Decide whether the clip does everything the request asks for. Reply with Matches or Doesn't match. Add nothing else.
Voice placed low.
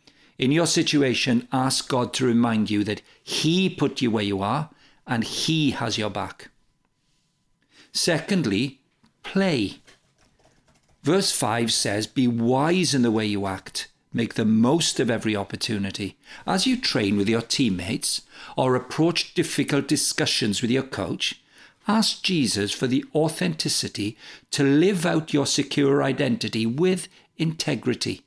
Matches